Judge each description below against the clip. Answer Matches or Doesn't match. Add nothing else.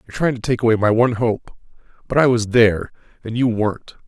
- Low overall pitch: Matches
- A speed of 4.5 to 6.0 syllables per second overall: Doesn't match